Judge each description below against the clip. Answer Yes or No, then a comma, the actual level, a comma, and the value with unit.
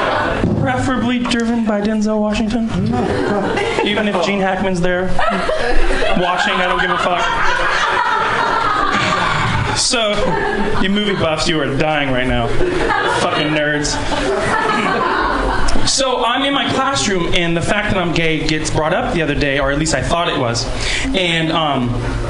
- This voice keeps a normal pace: Yes, average, 145 wpm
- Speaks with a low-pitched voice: No, medium, 180 Hz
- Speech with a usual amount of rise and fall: No, wide, 7.2 semitones